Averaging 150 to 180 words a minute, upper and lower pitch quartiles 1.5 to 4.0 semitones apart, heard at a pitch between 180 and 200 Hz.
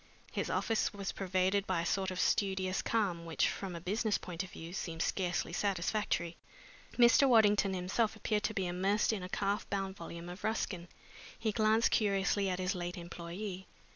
Yes: average, 175 wpm; average, 2.8 semitones; high, 190 Hz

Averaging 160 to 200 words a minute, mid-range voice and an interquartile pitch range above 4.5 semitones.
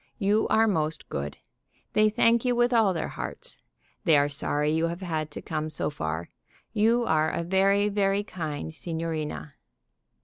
Yes: average, 165 wpm; medium, 170 Hz; average, 5.2 semitones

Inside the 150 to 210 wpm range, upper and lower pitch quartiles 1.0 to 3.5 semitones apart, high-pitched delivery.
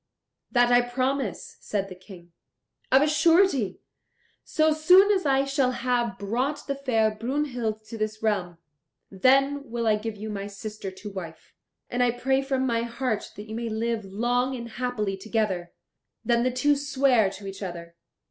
No: average, 170 wpm; average, 4.2 semitones; high, 235 Hz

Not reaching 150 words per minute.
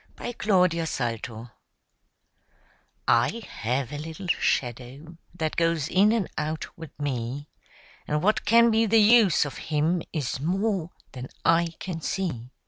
Yes: average, 140 wpm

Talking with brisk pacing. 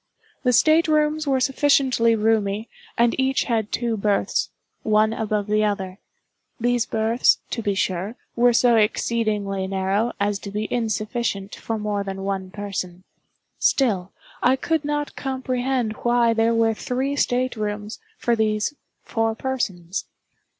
No: average, 140 wpm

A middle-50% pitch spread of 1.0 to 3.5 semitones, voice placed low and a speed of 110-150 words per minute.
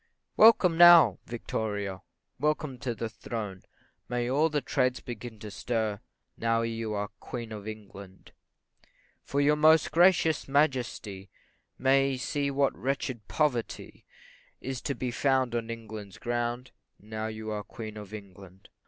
No: average, 4.2 semitones; low, 120 Hz; slow, 135 wpm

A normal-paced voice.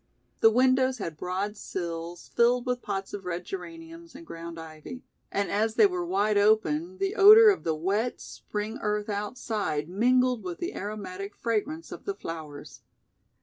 Yes: average, 160 wpm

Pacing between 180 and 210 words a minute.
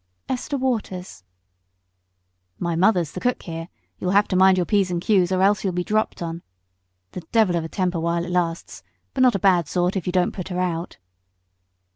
Yes: average, 200 wpm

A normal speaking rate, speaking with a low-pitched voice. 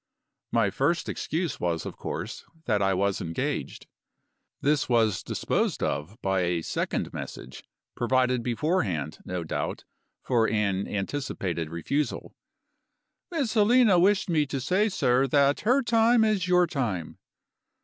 No: slow, 130 wpm; low, 125 Hz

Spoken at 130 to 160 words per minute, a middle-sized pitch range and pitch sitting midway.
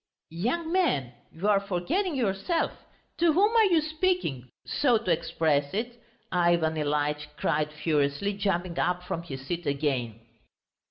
No: average, 140 wpm; wide, 9.0 semitones; medium, 175 Hz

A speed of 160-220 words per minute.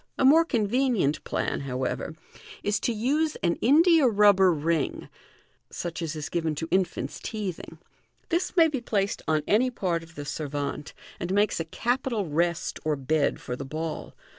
Yes: average, 165 wpm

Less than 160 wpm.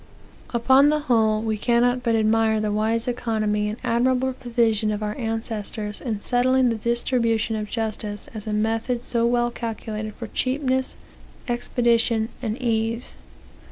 Yes: average, 145 wpm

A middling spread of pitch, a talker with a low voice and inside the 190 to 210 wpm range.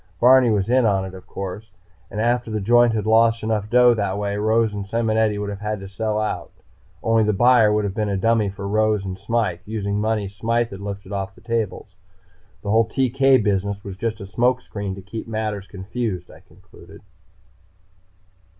No: narrow, 2.3 semitones; low, 105 Hz; average, 195 wpm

